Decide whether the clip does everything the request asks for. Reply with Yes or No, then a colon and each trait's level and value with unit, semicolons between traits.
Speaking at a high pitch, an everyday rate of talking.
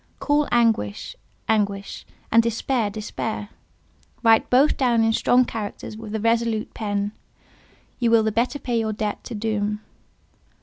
No: high, 225 Hz; slow, 130 wpm